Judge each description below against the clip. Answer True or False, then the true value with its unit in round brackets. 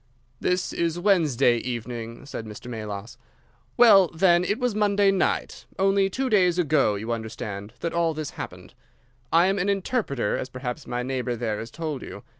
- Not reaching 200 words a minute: True (160 wpm)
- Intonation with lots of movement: True (8.2 semitones)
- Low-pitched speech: False (155 Hz)